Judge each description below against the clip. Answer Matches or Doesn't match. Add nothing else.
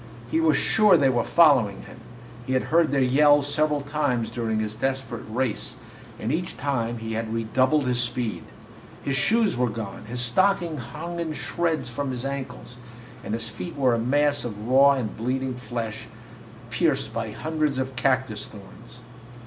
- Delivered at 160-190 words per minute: Matches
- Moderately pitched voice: Doesn't match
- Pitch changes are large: Doesn't match